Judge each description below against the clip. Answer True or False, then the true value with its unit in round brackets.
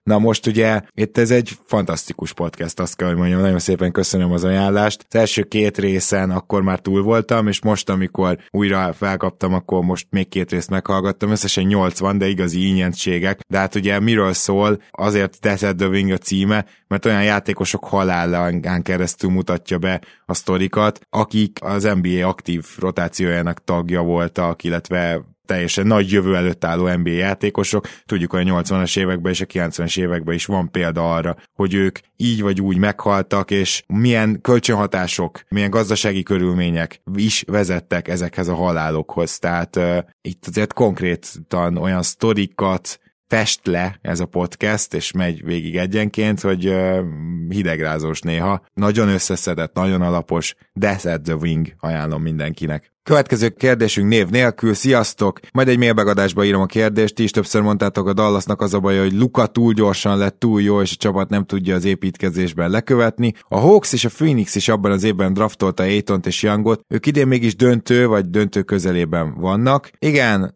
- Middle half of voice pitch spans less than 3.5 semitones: True (2.8 semitones)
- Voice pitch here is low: True (95 Hz)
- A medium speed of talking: False (165 wpm)